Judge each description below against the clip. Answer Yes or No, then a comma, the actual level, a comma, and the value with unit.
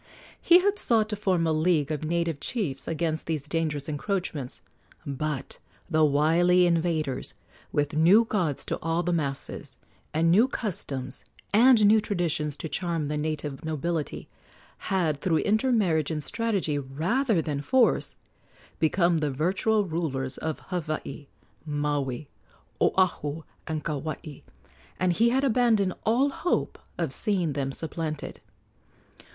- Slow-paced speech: Yes, slow, 130 wpm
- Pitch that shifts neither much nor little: Yes, average, 4.5 semitones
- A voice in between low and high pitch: Yes, medium, 165 Hz